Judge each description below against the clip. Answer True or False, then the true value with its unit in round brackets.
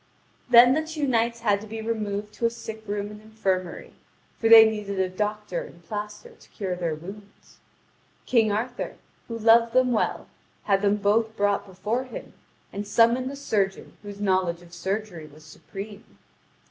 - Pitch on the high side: True (210 Hz)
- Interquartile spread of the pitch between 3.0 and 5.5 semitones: False (2.6 semitones)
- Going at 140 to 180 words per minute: True (170 wpm)